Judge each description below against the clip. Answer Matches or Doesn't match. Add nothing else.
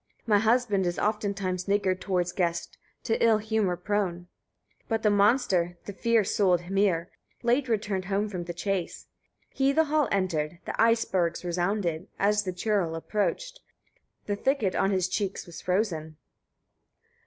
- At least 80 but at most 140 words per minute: Doesn't match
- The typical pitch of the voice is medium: Doesn't match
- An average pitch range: Matches